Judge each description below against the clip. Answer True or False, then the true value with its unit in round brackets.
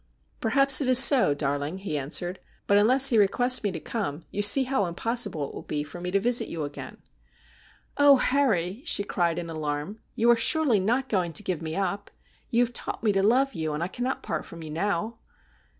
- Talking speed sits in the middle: False (230 wpm)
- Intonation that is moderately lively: False (6.5 semitones)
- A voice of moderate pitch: False (200 Hz)